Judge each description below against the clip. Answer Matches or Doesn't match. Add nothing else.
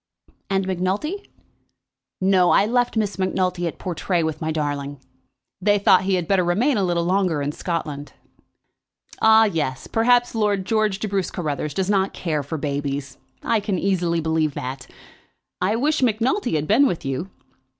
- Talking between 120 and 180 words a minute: Matches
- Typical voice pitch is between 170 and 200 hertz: Matches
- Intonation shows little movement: Doesn't match